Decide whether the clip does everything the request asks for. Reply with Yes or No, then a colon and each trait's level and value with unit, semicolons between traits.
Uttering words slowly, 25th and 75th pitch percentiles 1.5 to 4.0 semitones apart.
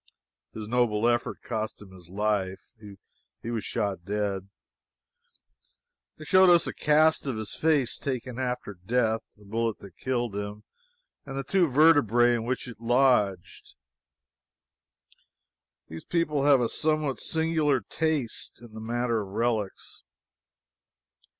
No: slow, 130 wpm; average, 4.6 semitones